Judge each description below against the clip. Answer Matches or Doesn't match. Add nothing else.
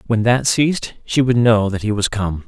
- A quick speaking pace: Matches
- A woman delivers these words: Doesn't match